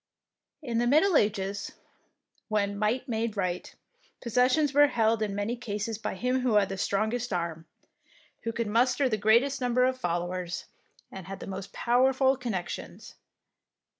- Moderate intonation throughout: Yes, average, 4.0 semitones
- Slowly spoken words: No, average, 155 wpm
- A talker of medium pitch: No, high, 225 Hz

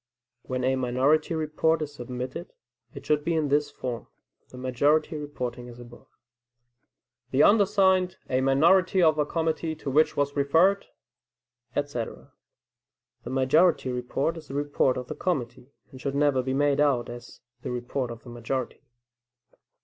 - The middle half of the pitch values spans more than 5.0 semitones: No, average, 3.7 semitones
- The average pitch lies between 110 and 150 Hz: Yes, medium, 140 Hz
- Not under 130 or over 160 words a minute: Yes, average, 150 wpm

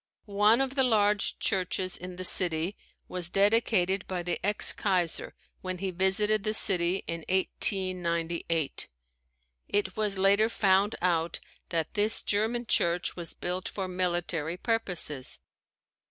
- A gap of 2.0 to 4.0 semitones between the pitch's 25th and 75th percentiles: Yes, average, 2.9 semitones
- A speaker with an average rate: No, slow, 130 wpm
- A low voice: No, medium, 185 Hz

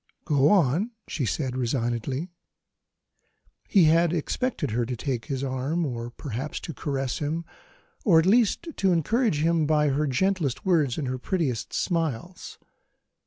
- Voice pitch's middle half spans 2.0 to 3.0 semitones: No, average, 4.8 semitones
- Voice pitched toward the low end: No, medium, 150 Hz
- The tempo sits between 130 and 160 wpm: Yes, average, 145 wpm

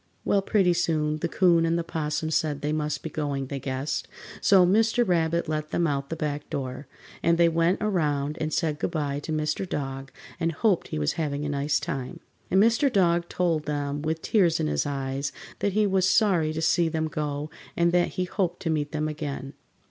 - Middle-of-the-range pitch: Yes, medium, 155 Hz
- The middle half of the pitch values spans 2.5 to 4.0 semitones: Yes, average, 3.0 semitones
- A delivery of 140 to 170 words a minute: No, fast, 205 wpm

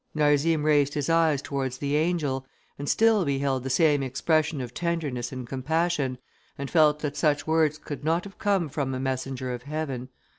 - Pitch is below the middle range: No, medium, 145 Hz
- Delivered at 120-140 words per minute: No, average, 180 wpm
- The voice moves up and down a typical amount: Yes, average, 3.1 semitones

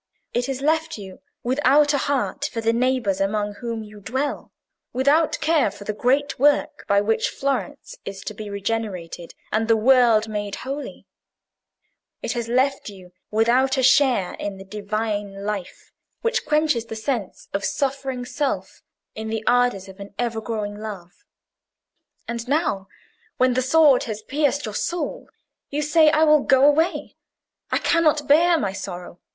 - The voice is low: No, high, 240 Hz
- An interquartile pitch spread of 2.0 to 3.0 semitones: No, wide, 5.4 semitones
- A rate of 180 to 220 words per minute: No, average, 160 wpm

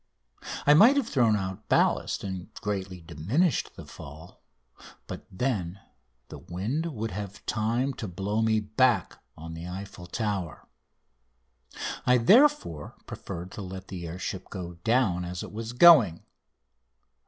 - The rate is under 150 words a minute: Yes, average, 140 wpm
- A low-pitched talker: Yes, low, 100 Hz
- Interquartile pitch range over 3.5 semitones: Yes, average, 5.2 semitones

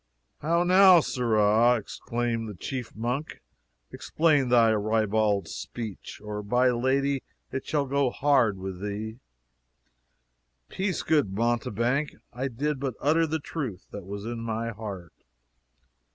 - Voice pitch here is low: Yes, low, 120 Hz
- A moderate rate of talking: No, slow, 125 wpm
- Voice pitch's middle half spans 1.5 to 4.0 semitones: No, average, 4.6 semitones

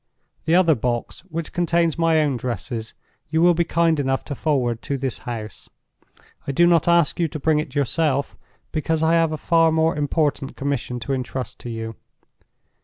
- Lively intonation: No, average, 3.9 semitones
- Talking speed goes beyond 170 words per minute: Yes, average, 180 wpm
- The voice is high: No, medium, 150 Hz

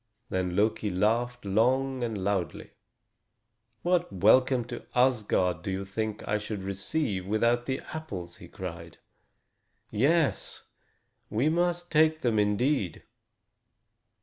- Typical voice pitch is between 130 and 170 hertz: No, low, 110 Hz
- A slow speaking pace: Yes, slow, 115 wpm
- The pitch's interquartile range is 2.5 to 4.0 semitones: No, average, 5.2 semitones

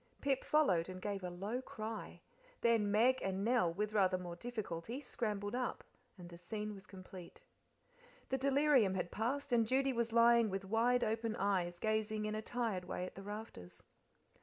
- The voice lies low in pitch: No, high, 215 Hz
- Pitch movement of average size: Yes, average, 3.9 semitones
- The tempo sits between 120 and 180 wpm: Yes, average, 175 wpm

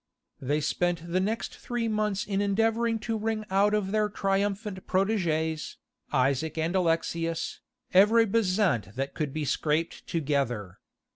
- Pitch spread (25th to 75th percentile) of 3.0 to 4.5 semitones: No, average, 5.1 semitones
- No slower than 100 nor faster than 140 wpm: Yes, slow, 135 wpm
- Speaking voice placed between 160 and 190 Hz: Yes, medium, 185 Hz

